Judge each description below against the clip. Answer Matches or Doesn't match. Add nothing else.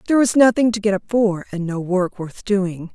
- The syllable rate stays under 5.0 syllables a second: Doesn't match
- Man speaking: Doesn't match